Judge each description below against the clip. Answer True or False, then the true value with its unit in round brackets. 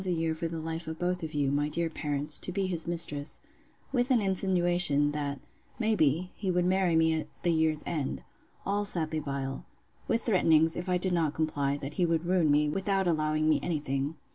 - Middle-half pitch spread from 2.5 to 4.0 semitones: True (3.2 semitones)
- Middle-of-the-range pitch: True (160 Hz)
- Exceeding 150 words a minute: True (205 wpm)